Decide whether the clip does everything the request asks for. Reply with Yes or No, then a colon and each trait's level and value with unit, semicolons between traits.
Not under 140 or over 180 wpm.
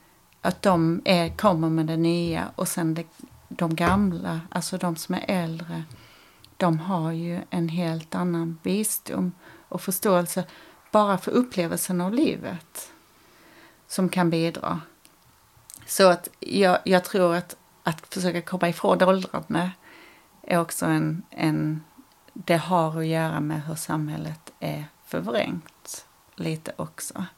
No: average, 130 wpm